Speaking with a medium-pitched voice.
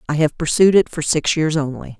Yes: medium, 155 Hz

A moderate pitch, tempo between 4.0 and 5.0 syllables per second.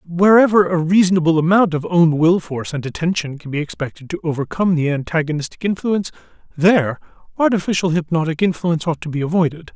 No: medium, 170 Hz; 6.3 syllables/s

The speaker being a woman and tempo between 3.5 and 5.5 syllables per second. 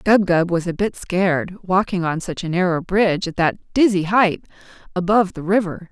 Yes: female; 5.1 syllables/s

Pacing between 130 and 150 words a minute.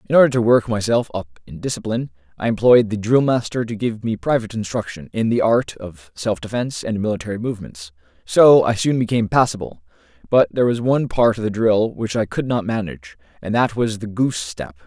No: average, 200 wpm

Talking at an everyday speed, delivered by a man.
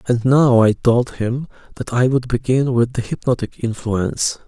Yes: average, 175 wpm; male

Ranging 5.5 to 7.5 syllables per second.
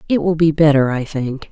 No: 5.3 syllables/s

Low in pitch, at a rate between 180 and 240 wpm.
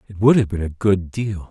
No: low, 100 Hz; fast, 280 wpm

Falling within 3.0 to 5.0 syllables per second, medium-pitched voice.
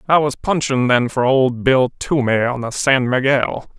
No: 4.4 syllables/s; low, 130 Hz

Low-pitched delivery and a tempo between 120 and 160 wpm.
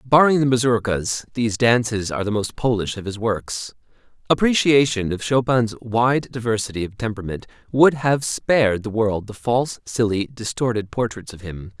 Yes: low, 115 Hz; average, 155 wpm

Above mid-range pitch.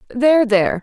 Yes: high, 245 Hz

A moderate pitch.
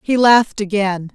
No: high, 210 Hz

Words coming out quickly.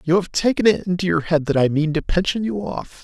Yes: fast, 275 wpm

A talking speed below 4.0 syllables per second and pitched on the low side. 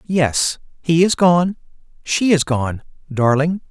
No: 3.4 syllables/s; medium, 155 Hz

